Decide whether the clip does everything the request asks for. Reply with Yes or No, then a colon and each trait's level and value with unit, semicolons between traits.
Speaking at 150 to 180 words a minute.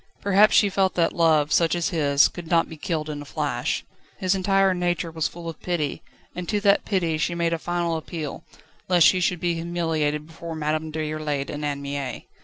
No: fast, 205 wpm